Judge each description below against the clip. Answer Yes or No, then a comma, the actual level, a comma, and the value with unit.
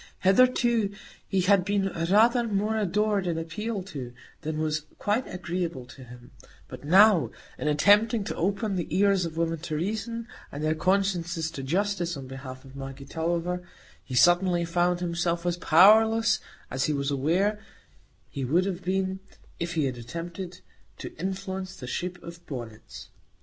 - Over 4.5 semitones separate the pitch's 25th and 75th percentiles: No, average, 4.2 semitones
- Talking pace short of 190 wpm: Yes, average, 160 wpm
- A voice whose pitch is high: No, medium, 175 Hz